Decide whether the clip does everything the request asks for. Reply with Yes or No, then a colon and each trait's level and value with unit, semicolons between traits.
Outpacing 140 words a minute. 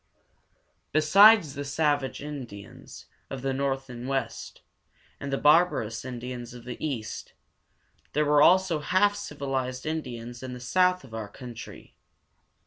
No: slow, 135 wpm